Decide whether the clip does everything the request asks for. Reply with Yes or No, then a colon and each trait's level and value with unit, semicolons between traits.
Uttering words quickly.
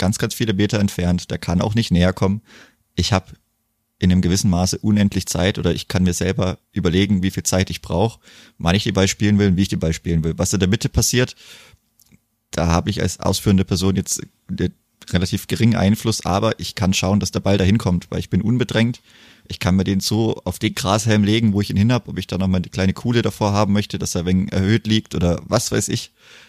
Yes: fast, 240 wpm